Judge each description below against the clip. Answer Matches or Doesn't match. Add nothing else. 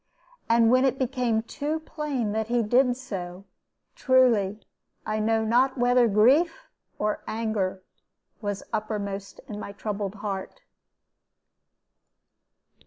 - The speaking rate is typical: Doesn't match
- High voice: Matches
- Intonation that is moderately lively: Matches